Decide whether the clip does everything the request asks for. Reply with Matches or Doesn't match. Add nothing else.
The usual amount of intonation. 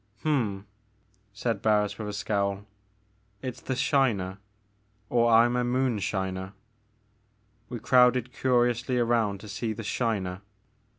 Matches